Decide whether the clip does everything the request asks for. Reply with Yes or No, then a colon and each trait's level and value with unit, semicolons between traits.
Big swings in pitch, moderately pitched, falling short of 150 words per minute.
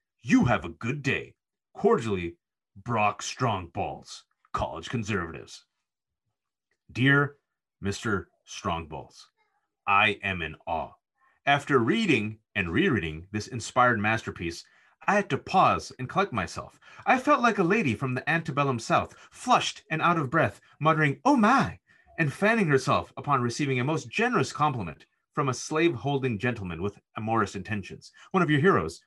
No: wide, 7.4 semitones; low, 130 Hz; average, 140 wpm